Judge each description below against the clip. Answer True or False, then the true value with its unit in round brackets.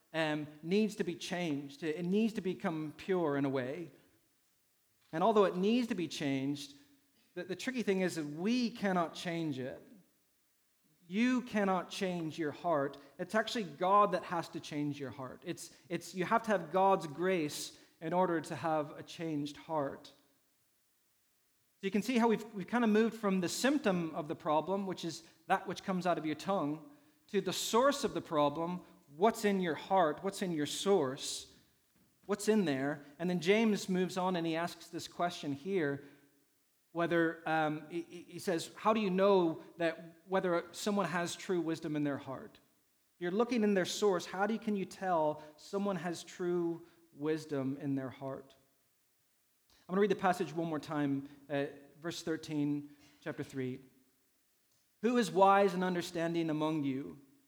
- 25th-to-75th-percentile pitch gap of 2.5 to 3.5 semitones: False (4.4 semitones)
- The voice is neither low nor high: True (170 Hz)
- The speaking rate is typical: True (175 wpm)